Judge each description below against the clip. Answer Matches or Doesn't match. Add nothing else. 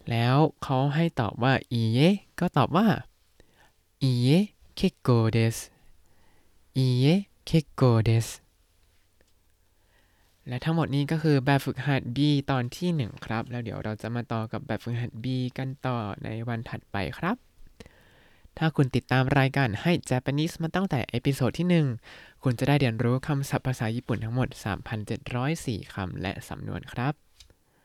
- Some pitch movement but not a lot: Matches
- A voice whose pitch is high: Doesn't match